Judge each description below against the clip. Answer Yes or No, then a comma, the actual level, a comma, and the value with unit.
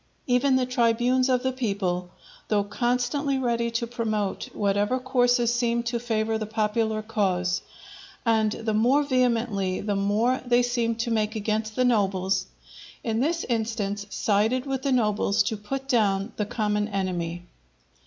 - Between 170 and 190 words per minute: No, average, 150 wpm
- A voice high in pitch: Yes, high, 225 Hz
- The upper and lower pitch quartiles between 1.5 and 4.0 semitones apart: Yes, average, 3.1 semitones